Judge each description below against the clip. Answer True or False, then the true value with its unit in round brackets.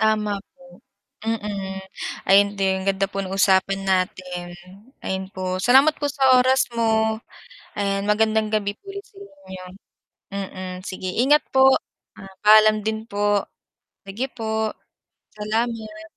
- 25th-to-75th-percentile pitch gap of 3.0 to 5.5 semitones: False (2.6 semitones)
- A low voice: False (210 Hz)